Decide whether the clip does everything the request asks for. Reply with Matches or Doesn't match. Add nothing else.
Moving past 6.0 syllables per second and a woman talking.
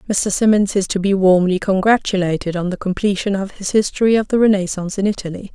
Matches